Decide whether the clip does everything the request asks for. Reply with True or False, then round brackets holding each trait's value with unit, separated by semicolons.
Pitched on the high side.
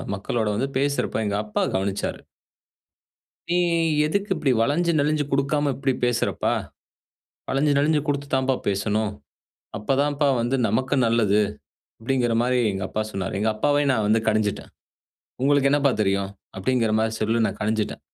False (120 Hz)